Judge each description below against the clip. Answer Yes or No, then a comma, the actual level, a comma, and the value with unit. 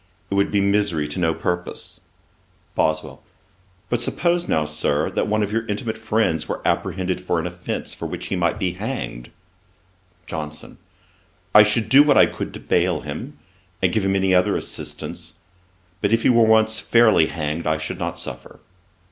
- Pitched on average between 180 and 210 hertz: No, very low, 95 Hz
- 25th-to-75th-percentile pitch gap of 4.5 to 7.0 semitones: Yes, average, 5.2 semitones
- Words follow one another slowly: No, average, 175 wpm